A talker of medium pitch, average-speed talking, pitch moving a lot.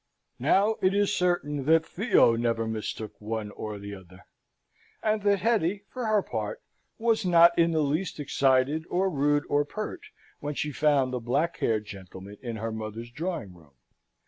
Yes: medium, 145 Hz; average, 165 wpm; wide, 8.3 semitones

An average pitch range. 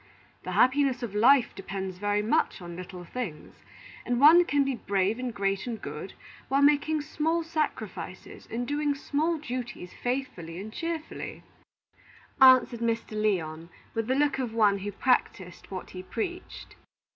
No: wide, 6.3 semitones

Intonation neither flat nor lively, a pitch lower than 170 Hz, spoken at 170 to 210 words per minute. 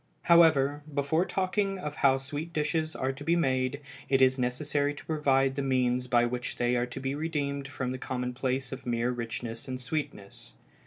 Yes: average, 3.0 semitones; low, 135 Hz; average, 180 wpm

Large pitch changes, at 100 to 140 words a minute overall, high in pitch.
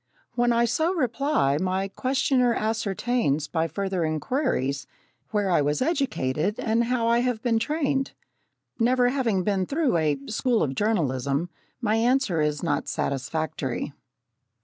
Yes: wide, 7.9 semitones; slow, 135 wpm; high, 215 Hz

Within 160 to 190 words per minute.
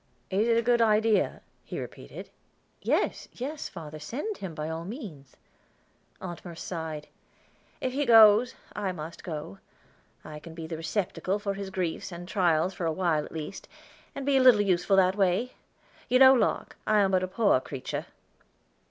Yes: average, 175 wpm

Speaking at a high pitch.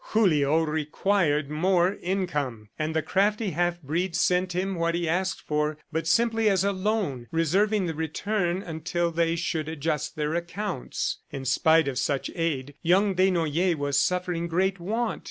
No: medium, 170 Hz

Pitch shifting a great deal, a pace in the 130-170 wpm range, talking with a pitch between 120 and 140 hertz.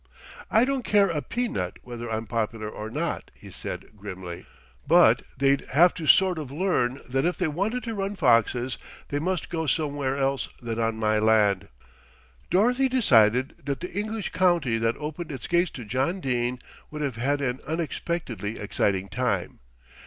Yes: wide, 7.5 semitones; average, 165 wpm; low, 135 Hz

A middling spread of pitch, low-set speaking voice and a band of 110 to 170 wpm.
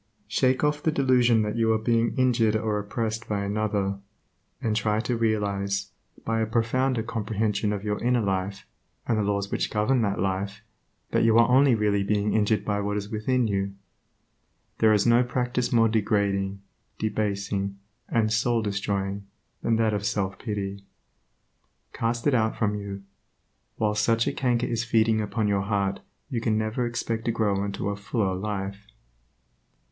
No: narrow, 2.3 semitones; low, 110 Hz; average, 165 wpm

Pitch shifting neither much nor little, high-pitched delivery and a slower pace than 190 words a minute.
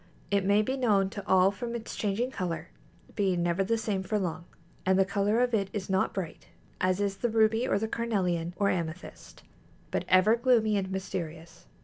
No: average, 3.0 semitones; high, 195 Hz; average, 195 wpm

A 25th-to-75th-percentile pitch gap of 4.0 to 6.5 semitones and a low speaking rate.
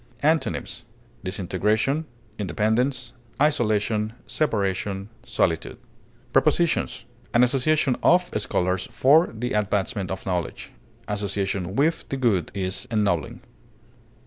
Yes: wide, 5.4 semitones; slow, 95 wpm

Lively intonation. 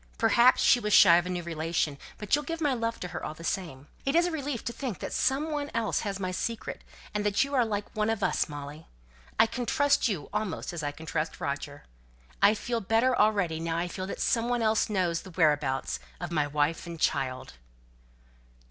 Yes: wide, 6.4 semitones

